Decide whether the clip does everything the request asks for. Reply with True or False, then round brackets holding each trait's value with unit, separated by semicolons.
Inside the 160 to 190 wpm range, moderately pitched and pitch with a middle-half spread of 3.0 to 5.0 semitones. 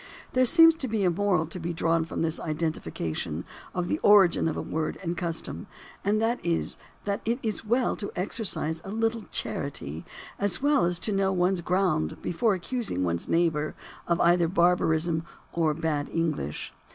True (175 wpm; 175 Hz; 4.3 semitones)